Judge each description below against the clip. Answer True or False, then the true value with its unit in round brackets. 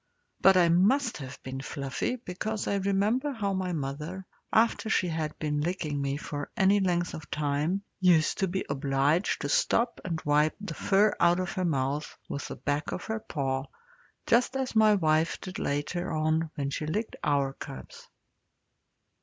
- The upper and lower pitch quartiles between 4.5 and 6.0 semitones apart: True (5.2 semitones)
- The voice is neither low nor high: True (170 Hz)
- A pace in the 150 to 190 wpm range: True (170 wpm)